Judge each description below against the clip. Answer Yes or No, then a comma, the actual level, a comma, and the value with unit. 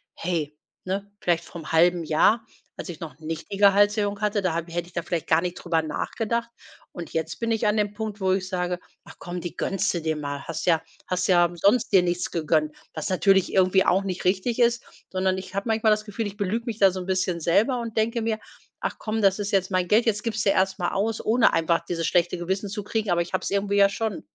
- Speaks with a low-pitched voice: No, high, 190 Hz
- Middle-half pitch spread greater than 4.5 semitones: No, average, 3.3 semitones